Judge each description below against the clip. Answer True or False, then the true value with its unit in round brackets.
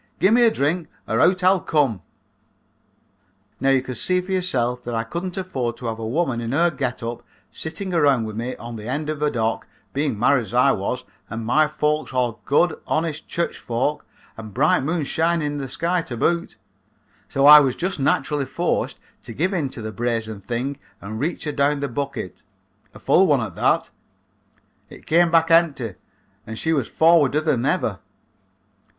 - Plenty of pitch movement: True (5.7 semitones)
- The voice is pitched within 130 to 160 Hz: True (140 Hz)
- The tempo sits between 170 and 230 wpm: True (190 wpm)